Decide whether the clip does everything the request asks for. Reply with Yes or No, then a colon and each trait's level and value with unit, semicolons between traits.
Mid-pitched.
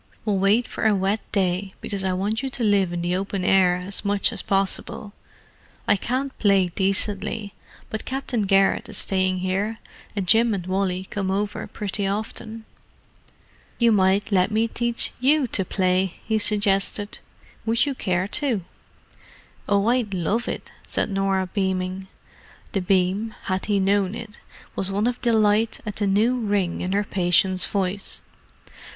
No: high, 200 Hz